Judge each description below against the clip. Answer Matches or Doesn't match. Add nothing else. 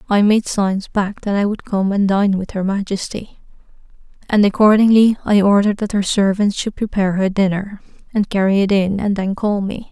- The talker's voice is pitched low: Doesn't match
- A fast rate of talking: Doesn't match